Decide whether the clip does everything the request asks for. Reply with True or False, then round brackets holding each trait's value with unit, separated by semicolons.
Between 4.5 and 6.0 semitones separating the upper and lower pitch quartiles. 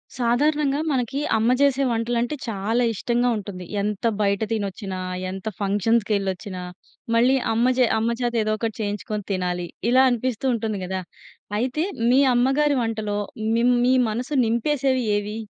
False (3.6 semitones)